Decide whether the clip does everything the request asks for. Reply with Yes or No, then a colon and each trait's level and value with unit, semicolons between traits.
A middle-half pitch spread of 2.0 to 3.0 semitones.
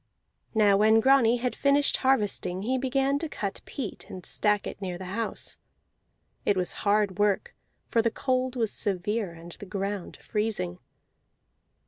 No: average, 4.3 semitones